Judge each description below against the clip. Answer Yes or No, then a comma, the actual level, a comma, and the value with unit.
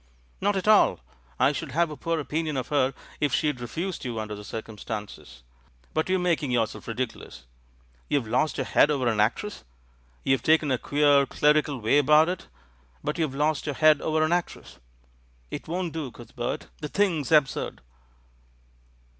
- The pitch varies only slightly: No, average, 4.3 semitones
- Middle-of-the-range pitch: Yes, medium, 150 Hz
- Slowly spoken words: No, average, 165 wpm